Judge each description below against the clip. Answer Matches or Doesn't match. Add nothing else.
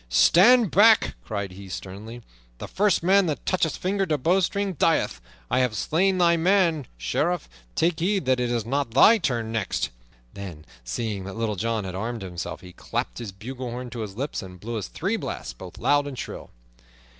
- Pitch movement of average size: Doesn't match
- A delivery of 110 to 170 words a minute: Doesn't match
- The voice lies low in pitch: Matches